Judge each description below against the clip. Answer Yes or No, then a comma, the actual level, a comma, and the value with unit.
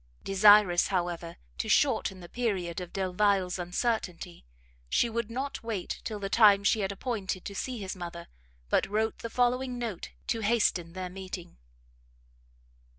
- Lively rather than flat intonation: No, average, 3.9 semitones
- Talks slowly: No, average, 150 wpm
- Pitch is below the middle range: No, high, 195 Hz